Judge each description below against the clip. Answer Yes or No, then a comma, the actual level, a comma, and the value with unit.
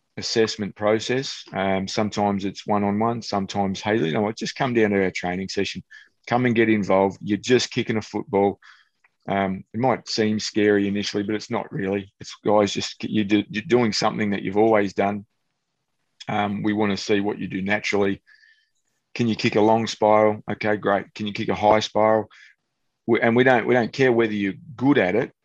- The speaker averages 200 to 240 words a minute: Yes, fast, 205 wpm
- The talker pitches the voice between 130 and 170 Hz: No, low, 105 Hz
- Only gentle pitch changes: Yes, narrow, 2.0 semitones